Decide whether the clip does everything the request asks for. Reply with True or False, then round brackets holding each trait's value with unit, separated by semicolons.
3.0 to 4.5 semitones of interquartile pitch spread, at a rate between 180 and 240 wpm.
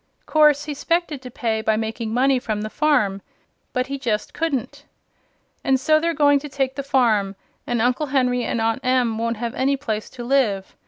True (3.8 semitones; 195 wpm)